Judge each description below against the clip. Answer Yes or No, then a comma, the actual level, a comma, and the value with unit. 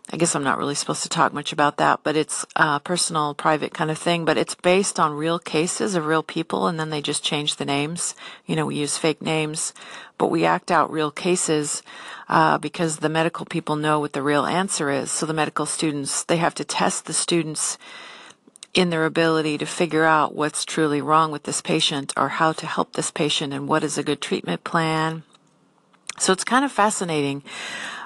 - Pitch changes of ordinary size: No, narrow, 1.8 semitones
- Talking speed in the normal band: No, fast, 210 wpm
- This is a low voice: No, medium, 155 Hz